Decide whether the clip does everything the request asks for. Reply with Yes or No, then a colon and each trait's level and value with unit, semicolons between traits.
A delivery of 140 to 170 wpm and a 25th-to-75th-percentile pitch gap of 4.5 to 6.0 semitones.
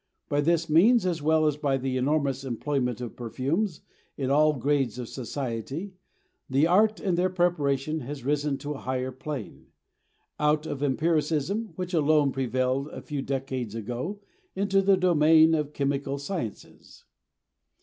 No: average, 150 wpm; average, 3.5 semitones